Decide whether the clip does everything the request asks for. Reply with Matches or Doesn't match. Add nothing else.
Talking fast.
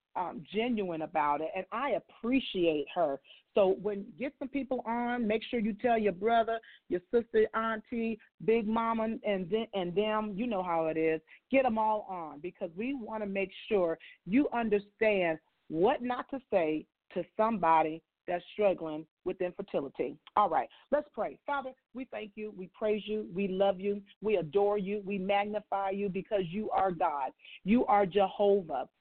Doesn't match